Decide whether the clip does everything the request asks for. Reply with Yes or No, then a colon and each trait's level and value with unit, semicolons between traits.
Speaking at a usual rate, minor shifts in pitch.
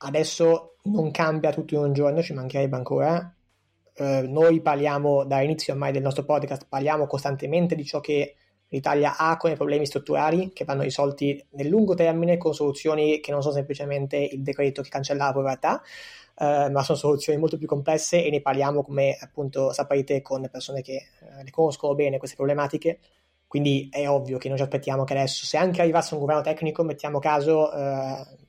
No: fast, 185 wpm; narrow, 2.1 semitones